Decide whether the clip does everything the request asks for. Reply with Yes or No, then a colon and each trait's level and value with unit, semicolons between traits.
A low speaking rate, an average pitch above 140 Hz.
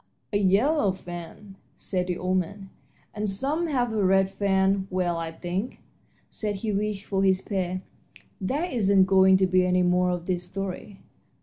No: average, 170 wpm; high, 190 Hz